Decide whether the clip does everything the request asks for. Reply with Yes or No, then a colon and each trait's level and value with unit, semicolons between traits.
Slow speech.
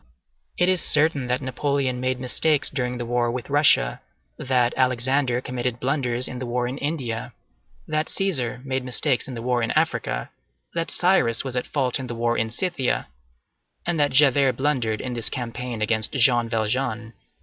No: average, 170 wpm